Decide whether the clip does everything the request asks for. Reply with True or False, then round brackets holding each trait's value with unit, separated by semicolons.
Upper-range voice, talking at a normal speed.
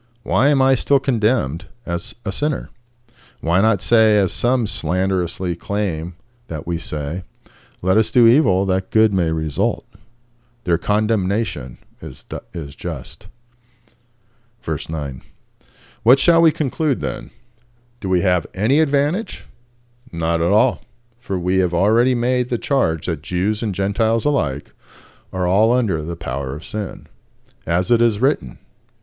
False (110 Hz; 145 wpm)